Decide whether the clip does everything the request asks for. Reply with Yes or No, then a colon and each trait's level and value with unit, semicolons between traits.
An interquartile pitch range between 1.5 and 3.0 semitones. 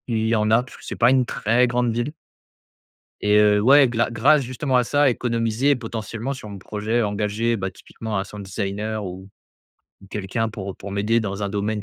Yes: narrow, 2.6 semitones